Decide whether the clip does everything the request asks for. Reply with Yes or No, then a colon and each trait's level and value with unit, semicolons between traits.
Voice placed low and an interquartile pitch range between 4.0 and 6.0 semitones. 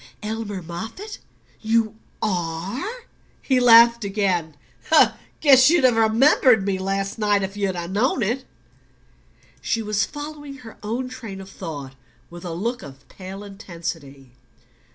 No: high, 210 Hz; average, 4.6 semitones